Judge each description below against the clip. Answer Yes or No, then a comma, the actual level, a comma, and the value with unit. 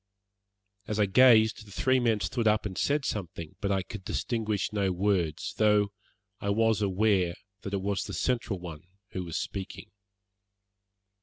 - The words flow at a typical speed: Yes, average, 160 wpm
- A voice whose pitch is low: Yes, low, 100 Hz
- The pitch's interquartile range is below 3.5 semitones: Yes, narrow, 2.6 semitones